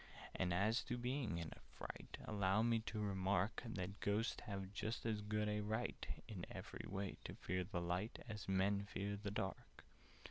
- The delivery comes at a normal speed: Yes, average, 185 wpm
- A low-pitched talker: Yes, low, 100 Hz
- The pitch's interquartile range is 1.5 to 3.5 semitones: Yes, narrow, 2.4 semitones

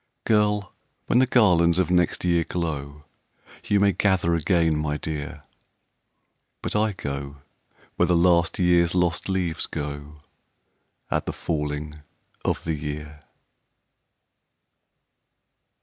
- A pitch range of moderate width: Yes, average, 3.3 semitones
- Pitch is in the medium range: No, very low, 85 Hz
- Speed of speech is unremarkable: No, slow, 115 wpm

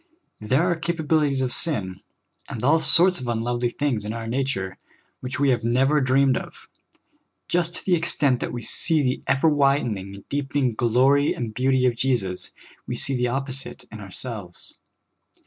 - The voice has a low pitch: Yes, low, 130 Hz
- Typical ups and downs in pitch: Yes, average, 3.6 semitones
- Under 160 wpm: No, average, 165 wpm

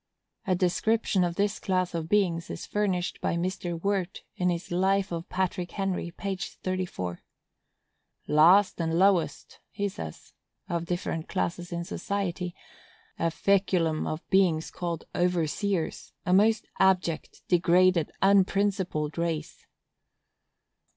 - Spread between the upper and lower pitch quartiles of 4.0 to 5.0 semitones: No, narrow, 2.4 semitones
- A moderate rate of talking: No, slow, 115 wpm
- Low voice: No, medium, 180 Hz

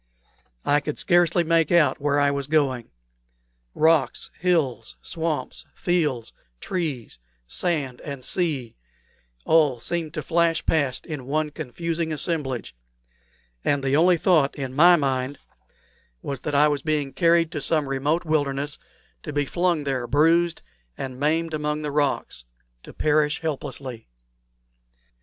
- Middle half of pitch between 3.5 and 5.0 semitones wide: No, average, 3.1 semitones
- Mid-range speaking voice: Yes, medium, 150 Hz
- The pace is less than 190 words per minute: Yes, slow, 135 wpm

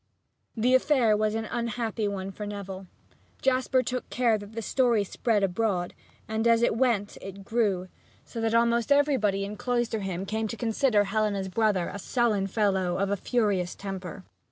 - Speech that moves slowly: No, average, 165 wpm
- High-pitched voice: Yes, high, 215 Hz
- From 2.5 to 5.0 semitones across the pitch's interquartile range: Yes, average, 3.0 semitones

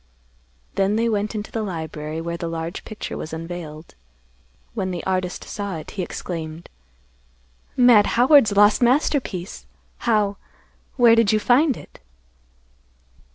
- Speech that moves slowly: Yes, slow, 125 wpm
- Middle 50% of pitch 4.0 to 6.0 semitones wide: Yes, average, 5.2 semitones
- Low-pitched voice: No, high, 200 Hz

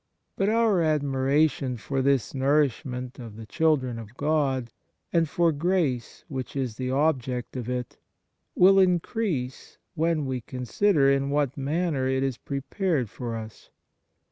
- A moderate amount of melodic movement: Yes, average, 3.9 semitones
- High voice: No, low, 135 Hz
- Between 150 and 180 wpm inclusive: No, average, 140 wpm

